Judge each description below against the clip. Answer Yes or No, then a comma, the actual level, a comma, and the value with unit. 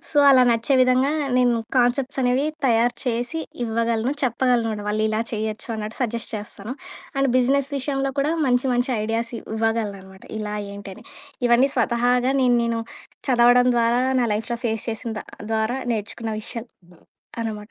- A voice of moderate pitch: No, high, 235 Hz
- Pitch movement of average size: No, narrow, 2.3 semitones